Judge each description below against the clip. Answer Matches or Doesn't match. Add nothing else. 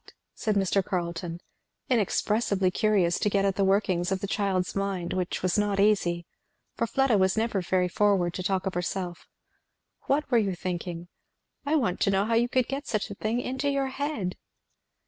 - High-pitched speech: Matches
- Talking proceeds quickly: Doesn't match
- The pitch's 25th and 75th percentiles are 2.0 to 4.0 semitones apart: Matches